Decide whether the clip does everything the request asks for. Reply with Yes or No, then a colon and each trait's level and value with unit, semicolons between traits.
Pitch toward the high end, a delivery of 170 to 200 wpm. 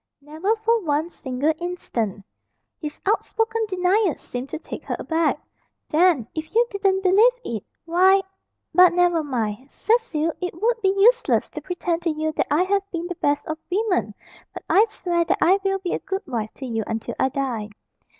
Yes: very high, 345 Hz; average, 180 wpm